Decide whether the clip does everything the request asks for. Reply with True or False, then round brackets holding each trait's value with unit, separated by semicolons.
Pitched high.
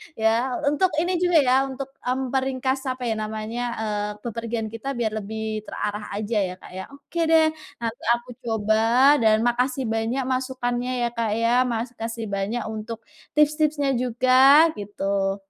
True (240 Hz)